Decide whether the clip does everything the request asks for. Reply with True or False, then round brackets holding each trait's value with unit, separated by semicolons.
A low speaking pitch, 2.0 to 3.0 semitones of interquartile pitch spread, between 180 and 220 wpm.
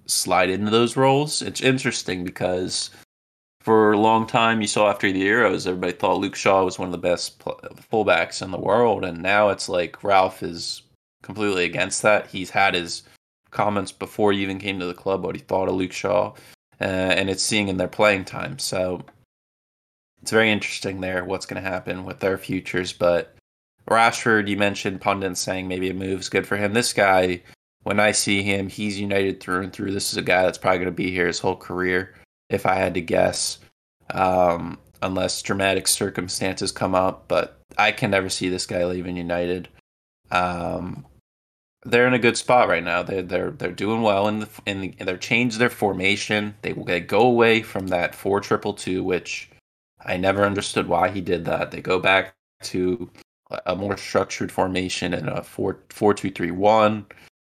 True (95 Hz; 2.7 semitones; 195 wpm)